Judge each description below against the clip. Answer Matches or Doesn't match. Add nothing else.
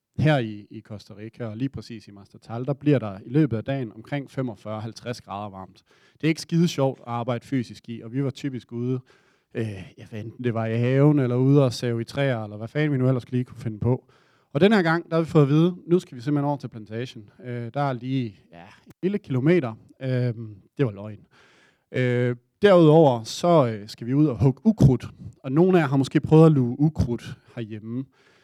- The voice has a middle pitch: Doesn't match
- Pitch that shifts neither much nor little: Matches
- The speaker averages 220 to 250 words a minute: Matches